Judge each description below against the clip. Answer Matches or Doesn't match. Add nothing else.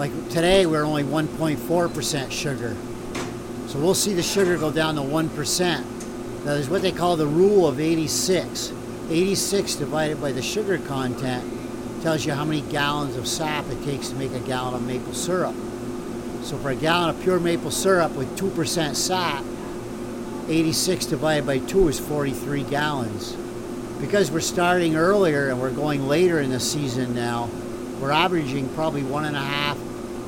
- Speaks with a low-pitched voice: Doesn't match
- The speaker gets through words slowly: Doesn't match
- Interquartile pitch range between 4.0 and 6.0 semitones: Matches